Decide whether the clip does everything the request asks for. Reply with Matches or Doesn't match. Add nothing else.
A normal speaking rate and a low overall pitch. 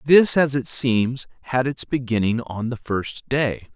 Matches